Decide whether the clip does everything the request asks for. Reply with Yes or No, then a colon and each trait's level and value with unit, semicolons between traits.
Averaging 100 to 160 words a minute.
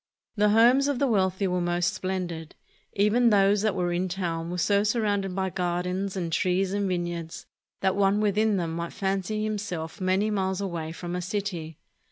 No: average, 180 wpm